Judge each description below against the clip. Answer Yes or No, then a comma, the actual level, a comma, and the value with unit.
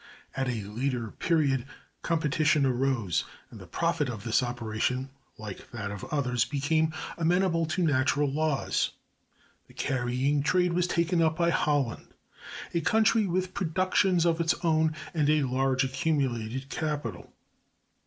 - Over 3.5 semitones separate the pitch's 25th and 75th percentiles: Yes, average, 4.6 semitones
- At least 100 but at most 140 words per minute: Yes, slow, 135 wpm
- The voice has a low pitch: No, medium, 145 Hz